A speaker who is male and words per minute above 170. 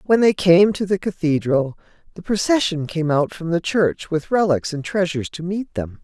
No: female; average, 200 wpm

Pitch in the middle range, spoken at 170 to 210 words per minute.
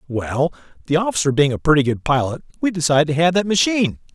Yes: medium, 155 Hz; fast, 205 wpm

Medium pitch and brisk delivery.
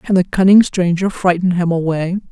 No: medium, 180 Hz; average, 180 wpm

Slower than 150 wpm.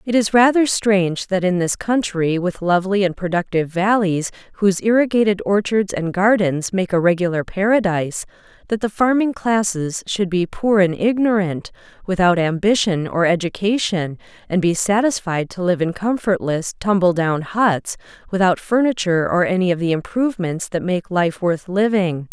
No: average, 155 wpm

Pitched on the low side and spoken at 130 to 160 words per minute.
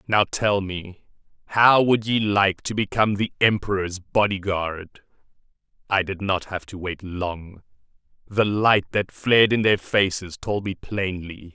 Yes: low, 100 Hz; average, 155 wpm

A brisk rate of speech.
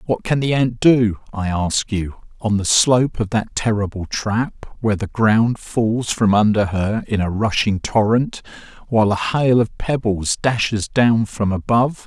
No: average, 175 wpm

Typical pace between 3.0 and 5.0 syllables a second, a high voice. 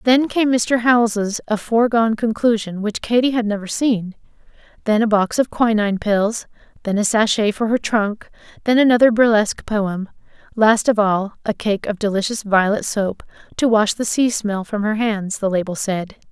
Yes: 4.9 syllables/s; high, 215 Hz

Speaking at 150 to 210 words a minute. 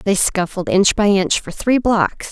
Yes: fast, 205 wpm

